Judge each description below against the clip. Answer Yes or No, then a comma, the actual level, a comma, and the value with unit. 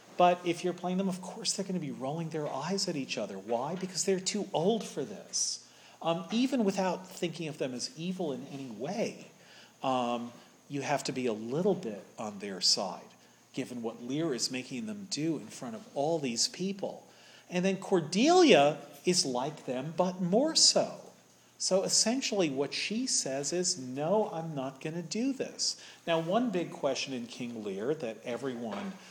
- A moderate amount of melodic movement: No, wide, 5.9 semitones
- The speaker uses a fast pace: No, average, 185 wpm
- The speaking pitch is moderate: Yes, medium, 175 Hz